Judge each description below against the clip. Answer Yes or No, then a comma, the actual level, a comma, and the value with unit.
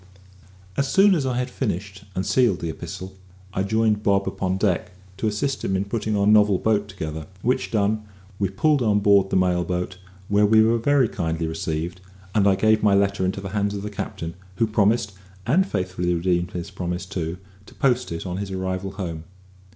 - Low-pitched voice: Yes, low, 100 Hz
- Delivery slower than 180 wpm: No, average, 195 wpm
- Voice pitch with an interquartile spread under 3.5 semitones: Yes, average, 2.9 semitones